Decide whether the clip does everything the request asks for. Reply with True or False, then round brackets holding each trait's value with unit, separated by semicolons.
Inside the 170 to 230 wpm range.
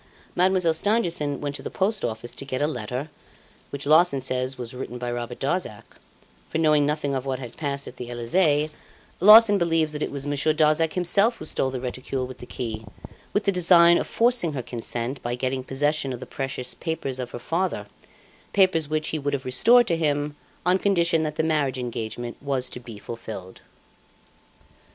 True (190 wpm)